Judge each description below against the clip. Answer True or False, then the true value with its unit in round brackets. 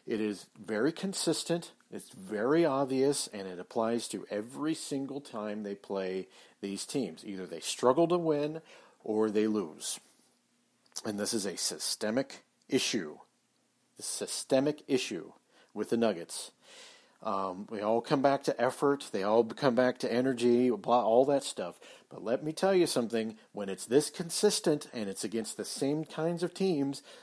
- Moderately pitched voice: False (130 Hz)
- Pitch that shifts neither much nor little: False (5.9 semitones)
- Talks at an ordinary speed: True (160 wpm)